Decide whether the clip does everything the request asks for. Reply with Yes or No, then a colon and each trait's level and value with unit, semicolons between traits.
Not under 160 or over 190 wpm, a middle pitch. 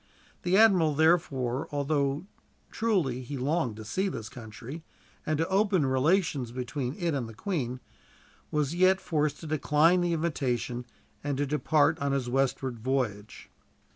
No: average, 150 wpm; medium, 145 Hz